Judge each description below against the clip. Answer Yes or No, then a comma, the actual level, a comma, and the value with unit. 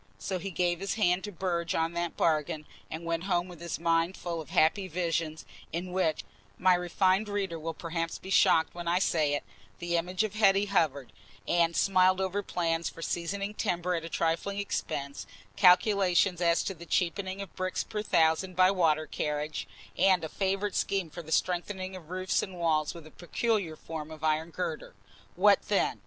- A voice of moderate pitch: Yes, medium, 175 Hz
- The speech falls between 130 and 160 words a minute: No, average, 185 wpm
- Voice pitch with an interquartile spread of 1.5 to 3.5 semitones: Yes, narrow, 2.5 semitones